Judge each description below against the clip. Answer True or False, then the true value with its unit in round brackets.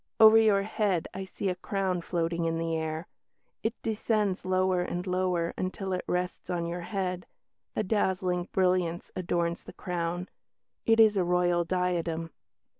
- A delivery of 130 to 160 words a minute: True (155 wpm)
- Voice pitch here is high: False (180 Hz)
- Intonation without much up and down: True (1.9 semitones)